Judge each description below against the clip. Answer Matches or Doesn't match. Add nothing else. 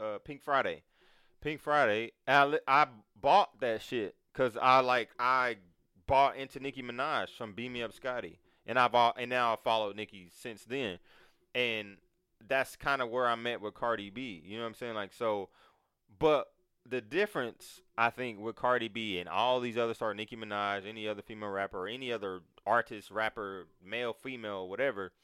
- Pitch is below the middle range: Matches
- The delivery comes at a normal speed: Matches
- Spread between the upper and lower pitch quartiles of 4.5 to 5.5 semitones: Doesn't match